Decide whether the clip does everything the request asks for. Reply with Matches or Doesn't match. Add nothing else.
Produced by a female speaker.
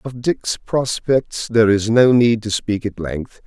Doesn't match